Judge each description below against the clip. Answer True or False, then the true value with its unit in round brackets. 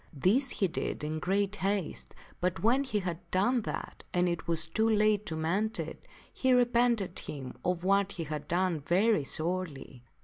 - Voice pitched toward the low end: False (185 Hz)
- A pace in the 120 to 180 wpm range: True (175 wpm)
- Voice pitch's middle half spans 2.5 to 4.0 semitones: False (4.4 semitones)